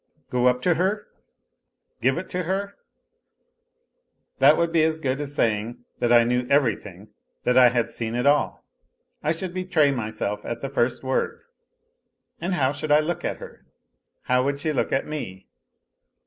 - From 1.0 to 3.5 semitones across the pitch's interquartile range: No, average, 4.7 semitones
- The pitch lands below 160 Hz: Yes, low, 135 Hz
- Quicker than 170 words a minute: No, average, 165 wpm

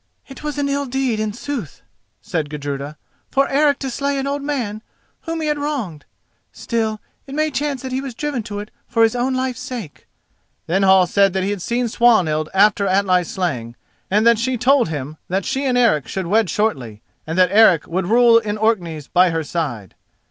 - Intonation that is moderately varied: No, wide, 6.8 semitones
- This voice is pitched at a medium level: No, high, 215 Hz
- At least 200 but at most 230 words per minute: Yes, fast, 205 wpm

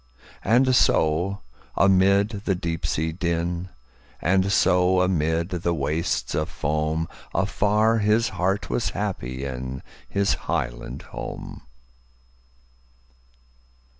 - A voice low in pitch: Yes, very low, 90 Hz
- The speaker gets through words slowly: Yes, slow, 85 wpm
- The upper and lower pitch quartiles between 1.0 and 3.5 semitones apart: No, average, 4.0 semitones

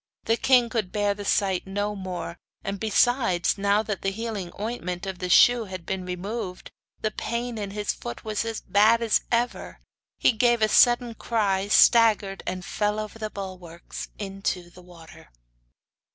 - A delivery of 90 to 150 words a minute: No, average, 165 wpm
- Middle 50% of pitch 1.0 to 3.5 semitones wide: Yes, average, 3.2 semitones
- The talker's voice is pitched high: Yes, high, 205 Hz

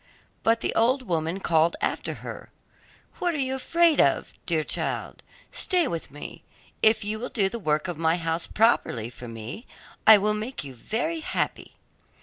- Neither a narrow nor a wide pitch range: No, wide, 7.3 semitones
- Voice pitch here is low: No, high, 205 Hz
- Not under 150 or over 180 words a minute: Yes, average, 170 wpm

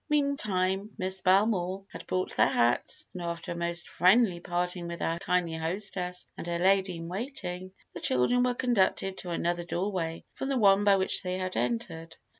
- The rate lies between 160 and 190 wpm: Yes, average, 180 wpm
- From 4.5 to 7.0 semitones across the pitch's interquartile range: No, narrow, 2.4 semitones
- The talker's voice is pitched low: No, medium, 185 Hz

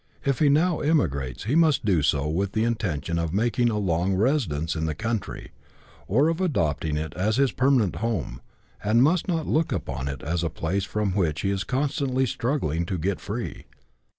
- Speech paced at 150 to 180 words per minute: No, average, 190 wpm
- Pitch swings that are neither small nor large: No, wide, 8.2 semitones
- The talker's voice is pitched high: No, low, 100 Hz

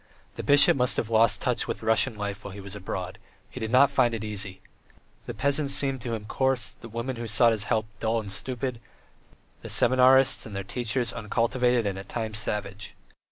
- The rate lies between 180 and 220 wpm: Yes, average, 200 wpm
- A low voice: Yes, low, 115 Hz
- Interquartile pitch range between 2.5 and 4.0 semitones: Yes, average, 3.4 semitones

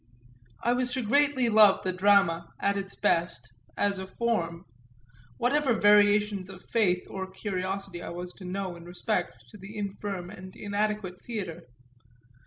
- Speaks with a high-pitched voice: Yes, high, 195 Hz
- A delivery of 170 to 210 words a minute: No, average, 150 wpm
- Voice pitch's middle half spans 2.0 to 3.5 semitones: Yes, average, 2.8 semitones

